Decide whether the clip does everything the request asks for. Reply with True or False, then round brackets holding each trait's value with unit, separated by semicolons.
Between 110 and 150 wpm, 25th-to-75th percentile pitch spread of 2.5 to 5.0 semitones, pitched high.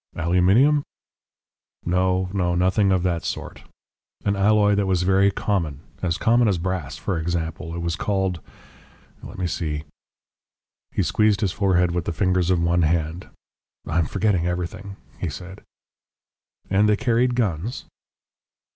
False (145 wpm; 2.8 semitones; 90 Hz)